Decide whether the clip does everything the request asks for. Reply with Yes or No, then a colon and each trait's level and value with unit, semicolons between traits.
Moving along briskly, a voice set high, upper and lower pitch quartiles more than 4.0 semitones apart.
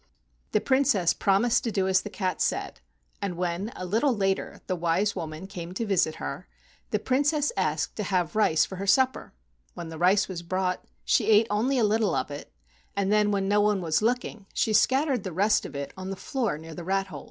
No: fast, 215 wpm; high, 195 Hz; average, 3.5 semitones